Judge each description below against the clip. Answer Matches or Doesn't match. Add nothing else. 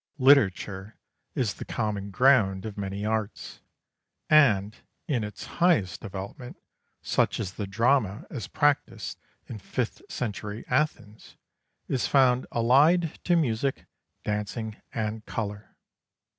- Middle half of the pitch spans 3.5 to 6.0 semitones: Matches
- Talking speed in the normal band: Doesn't match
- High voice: Doesn't match